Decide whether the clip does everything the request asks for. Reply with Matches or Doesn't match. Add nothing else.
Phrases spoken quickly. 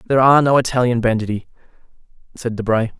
Doesn't match